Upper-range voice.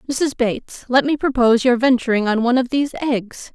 Yes: very high, 250 Hz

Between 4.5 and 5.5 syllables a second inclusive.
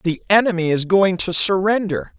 Yes: 4.8 syllables/s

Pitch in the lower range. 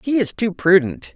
No: high, 195 Hz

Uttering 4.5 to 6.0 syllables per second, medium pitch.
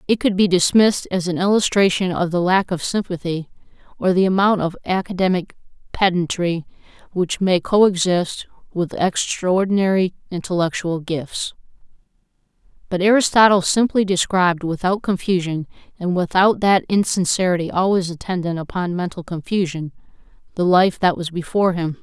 Yes: 5.1 syllables/s; medium, 180 Hz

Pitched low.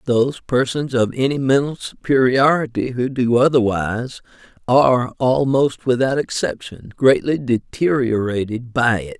Yes: low, 125 Hz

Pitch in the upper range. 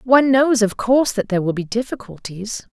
Yes: high, 225 Hz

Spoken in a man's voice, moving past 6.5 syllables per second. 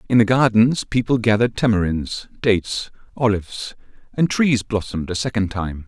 No: male; 5.3 syllables/s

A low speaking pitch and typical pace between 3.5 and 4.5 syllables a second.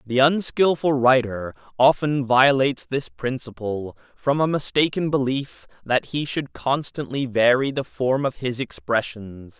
Yes: low, 130 Hz; 4.2 syllables/s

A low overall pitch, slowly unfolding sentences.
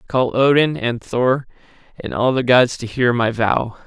No: low, 125 Hz; average, 200 wpm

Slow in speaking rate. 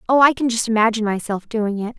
No: fast, 240 wpm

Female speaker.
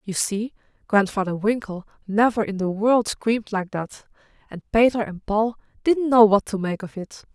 Yes: female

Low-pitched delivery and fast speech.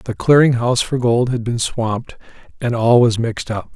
Yes: low, 120 Hz; fast, 210 wpm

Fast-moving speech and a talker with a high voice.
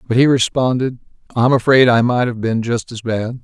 No: fast, 210 wpm; low, 120 Hz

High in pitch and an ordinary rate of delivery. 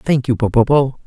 No: low, 130 Hz; average, 170 wpm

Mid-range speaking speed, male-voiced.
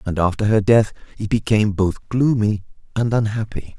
Yes: average, 160 wpm; male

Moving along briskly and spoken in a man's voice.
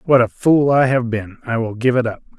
Yes: fast, 275 wpm; male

